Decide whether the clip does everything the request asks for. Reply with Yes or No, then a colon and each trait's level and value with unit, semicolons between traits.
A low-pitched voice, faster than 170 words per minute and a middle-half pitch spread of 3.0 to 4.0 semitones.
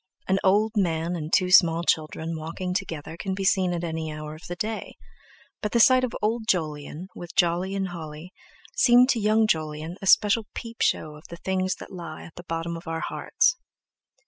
No: medium, 175 Hz; average, 200 wpm; average, 3.7 semitones